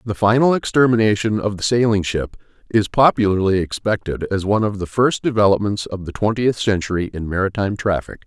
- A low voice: Yes, low, 105 Hz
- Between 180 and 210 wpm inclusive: No, average, 165 wpm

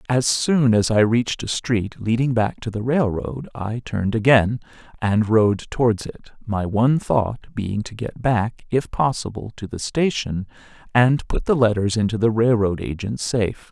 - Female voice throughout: No, male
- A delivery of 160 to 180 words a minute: Yes, average, 175 wpm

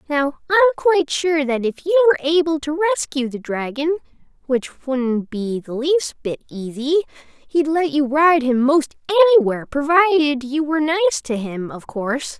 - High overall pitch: Yes, very high, 295 Hz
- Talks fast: No, average, 170 wpm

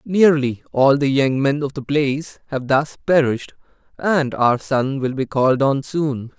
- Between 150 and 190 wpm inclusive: Yes, average, 180 wpm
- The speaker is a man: Yes, male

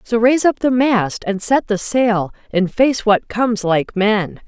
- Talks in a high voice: Yes, high, 220 Hz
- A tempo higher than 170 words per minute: Yes, average, 200 wpm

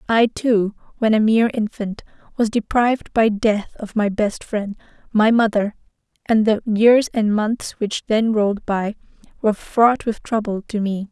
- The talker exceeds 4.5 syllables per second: No, 4.4 syllables/s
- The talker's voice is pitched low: No, high, 215 Hz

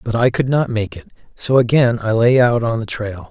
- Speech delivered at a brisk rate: Yes, fast, 255 wpm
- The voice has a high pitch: No, low, 115 Hz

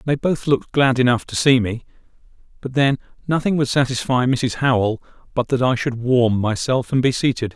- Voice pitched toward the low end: Yes, low, 125 Hz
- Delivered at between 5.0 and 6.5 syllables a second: Yes, 5.3 syllables/s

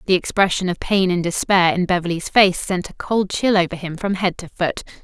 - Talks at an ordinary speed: No, fast, 225 wpm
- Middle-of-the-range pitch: Yes, medium, 180 Hz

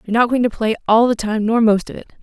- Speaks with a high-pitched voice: Yes, high, 225 Hz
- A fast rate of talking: Yes, fast, 325 wpm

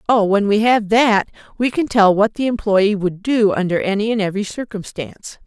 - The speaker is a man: No, female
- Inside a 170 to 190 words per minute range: No, average, 200 wpm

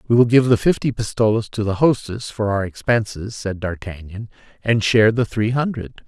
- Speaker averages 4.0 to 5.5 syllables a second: Yes, 5.3 syllables/s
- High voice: No, low, 110 Hz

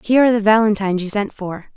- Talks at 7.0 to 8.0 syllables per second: Yes, 7.3 syllables/s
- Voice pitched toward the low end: No, high, 210 Hz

